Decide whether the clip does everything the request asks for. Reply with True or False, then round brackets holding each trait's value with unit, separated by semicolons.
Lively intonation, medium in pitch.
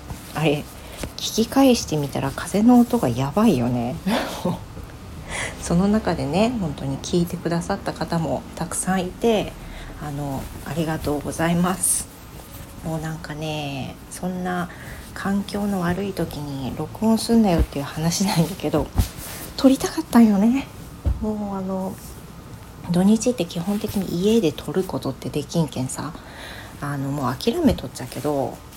True (6.1 semitones; 170 Hz)